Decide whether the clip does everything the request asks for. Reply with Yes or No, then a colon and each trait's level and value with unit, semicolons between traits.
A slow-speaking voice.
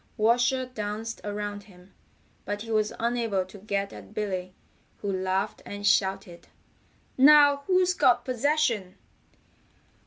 Yes: slow, 120 wpm